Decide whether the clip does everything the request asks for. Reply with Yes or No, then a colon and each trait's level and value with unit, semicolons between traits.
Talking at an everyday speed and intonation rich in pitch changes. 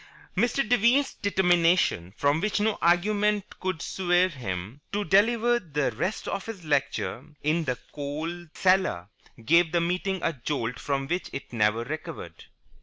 Yes: average, 145 wpm; wide, 5.7 semitones